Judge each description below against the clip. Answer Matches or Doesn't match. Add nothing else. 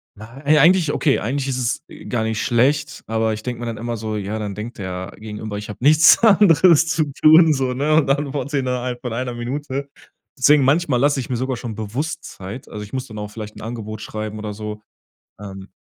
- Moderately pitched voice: Doesn't match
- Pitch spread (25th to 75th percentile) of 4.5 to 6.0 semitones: Matches